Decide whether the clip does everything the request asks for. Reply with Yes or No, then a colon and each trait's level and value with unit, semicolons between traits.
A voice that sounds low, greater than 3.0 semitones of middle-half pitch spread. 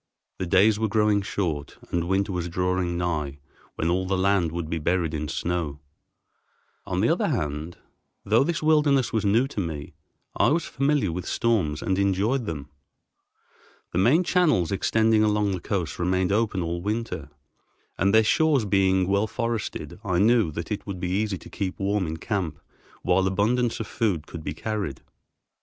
Yes: very low, 95 Hz; average, 4.1 semitones